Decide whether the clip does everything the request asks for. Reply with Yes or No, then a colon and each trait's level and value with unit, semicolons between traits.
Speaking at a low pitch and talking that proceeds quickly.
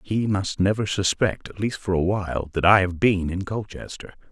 Yes: very low, 95 Hz; fast, 210 wpm